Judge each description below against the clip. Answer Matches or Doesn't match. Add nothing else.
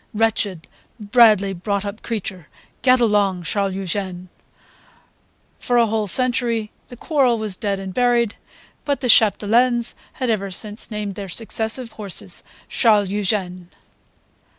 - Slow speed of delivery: Matches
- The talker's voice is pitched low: Doesn't match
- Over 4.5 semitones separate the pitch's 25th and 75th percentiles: Doesn't match